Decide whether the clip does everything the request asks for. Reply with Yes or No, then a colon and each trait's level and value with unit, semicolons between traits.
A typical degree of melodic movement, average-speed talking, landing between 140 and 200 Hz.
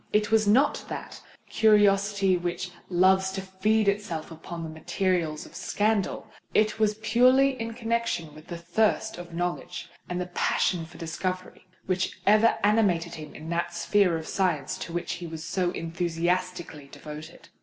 Yes: average, 3.8 semitones; average, 155 wpm; medium, 185 Hz